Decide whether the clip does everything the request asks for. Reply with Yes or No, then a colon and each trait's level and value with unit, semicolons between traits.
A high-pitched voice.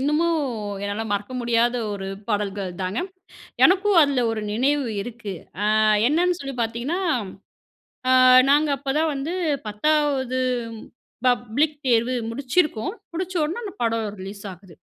Yes: very high, 255 Hz